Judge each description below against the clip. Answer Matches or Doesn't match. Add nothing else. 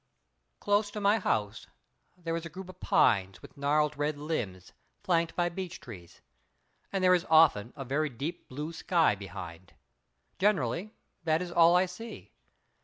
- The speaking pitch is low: Doesn't match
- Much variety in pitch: Matches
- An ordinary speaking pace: Matches